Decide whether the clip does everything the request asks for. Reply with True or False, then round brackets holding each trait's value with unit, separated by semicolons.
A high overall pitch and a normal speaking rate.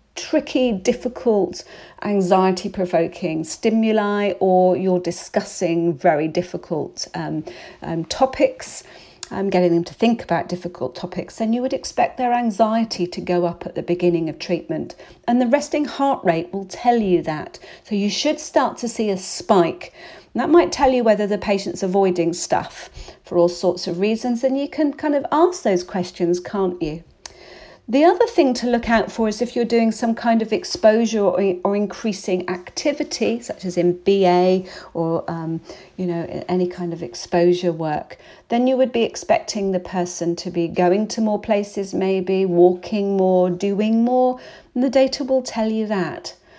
True (200 Hz; 170 wpm)